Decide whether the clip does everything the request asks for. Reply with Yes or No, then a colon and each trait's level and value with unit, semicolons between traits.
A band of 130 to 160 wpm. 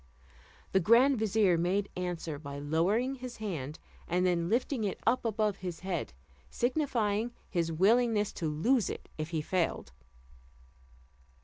Yes: slow, 135 wpm